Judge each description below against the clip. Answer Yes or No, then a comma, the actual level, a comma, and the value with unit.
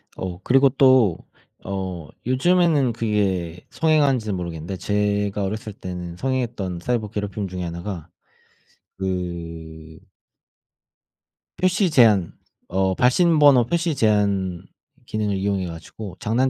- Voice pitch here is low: Yes, low, 100 Hz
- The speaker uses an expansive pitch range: Yes, wide, 5.8 semitones